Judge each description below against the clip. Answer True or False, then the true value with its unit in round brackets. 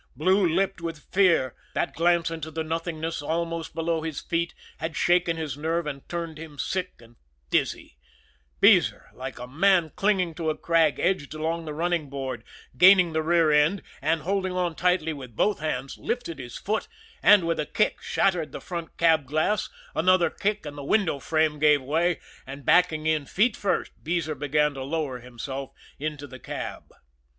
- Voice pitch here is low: False (160 Hz)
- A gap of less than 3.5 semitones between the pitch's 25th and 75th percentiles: True (2.9 semitones)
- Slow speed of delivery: False (175 wpm)